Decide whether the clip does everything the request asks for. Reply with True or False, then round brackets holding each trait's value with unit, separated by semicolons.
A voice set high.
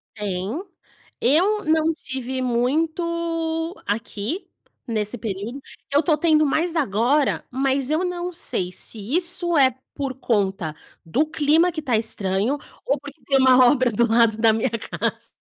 True (270 Hz)